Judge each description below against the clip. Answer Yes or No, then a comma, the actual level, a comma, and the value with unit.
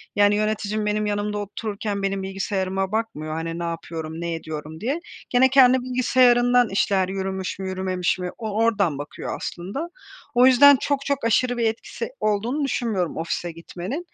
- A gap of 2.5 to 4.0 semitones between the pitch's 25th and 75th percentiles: No, average, 4.6 semitones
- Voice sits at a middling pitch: No, high, 205 Hz